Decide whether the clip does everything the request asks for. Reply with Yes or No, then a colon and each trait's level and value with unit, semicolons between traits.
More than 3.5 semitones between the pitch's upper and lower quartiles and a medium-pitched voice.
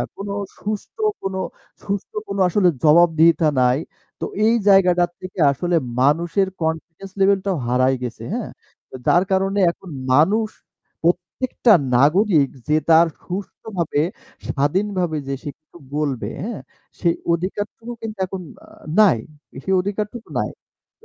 Yes: average, 4.1 semitones; medium, 180 Hz